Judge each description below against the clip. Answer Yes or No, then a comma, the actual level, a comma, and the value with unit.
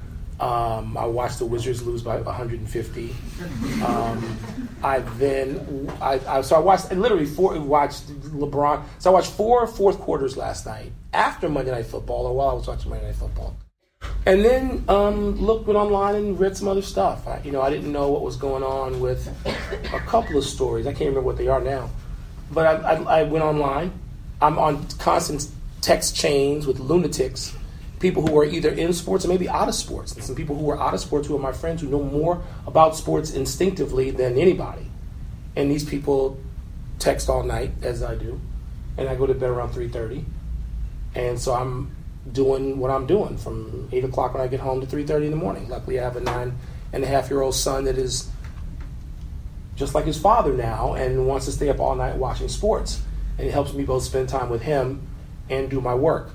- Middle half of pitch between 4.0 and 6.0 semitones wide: No, average, 3.3 semitones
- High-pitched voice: No, low, 135 Hz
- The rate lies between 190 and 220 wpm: Yes, fast, 205 wpm